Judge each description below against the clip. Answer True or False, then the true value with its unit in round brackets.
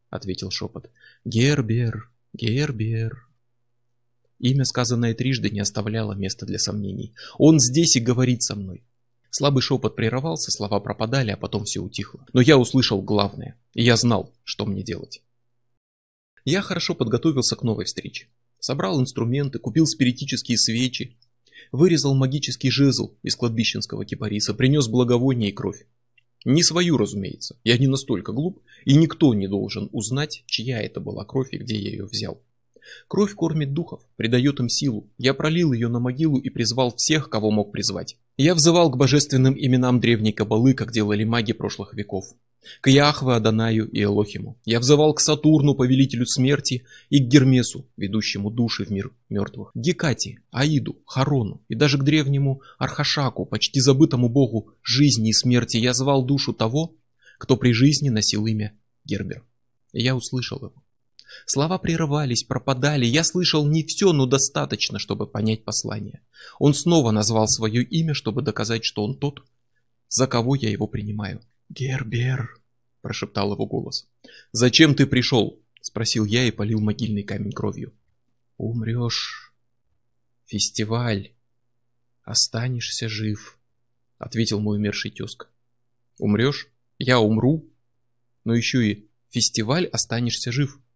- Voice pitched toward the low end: True (120 Hz)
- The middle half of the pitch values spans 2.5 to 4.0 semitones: True (3.6 semitones)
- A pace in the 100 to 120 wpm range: False (140 wpm)